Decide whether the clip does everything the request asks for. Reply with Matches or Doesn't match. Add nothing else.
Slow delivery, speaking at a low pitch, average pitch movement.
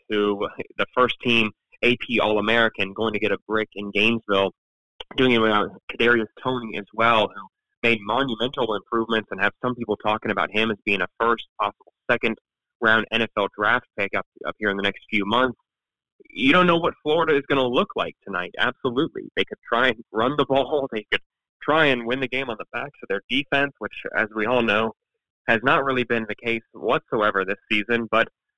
Doesn't match